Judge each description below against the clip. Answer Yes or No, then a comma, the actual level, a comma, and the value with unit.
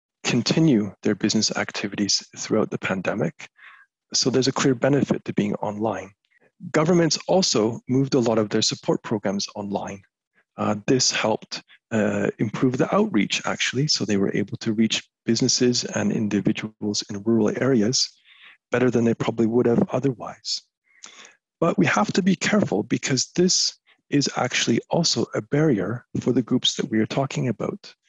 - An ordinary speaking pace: Yes, average, 155 wpm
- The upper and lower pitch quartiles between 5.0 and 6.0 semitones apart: No, average, 4.6 semitones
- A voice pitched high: No, low, 120 Hz